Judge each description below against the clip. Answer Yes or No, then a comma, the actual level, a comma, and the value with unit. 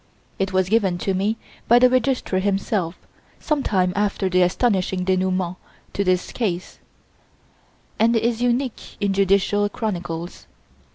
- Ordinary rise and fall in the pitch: Yes, average, 3.4 semitones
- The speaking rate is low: Yes, slow, 130 wpm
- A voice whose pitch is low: No, high, 195 Hz